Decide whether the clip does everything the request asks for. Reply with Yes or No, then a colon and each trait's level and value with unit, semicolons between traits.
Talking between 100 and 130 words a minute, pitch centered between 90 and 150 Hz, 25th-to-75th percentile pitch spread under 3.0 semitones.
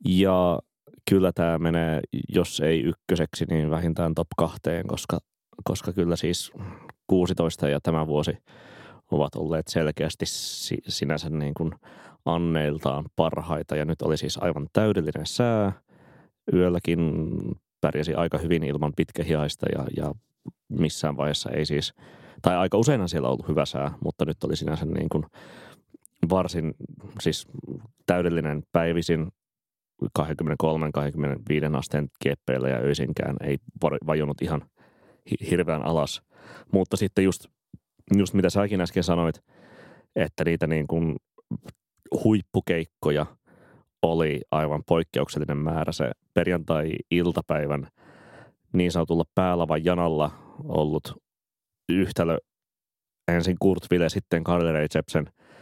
No: average, 110 wpm; very low, 80 Hz; narrow, 2.5 semitones